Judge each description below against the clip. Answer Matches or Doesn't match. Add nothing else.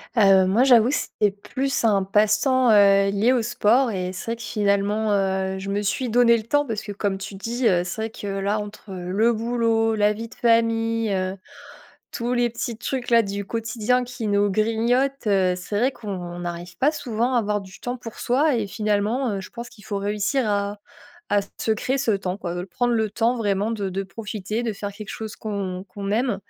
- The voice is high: Matches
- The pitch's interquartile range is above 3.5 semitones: Doesn't match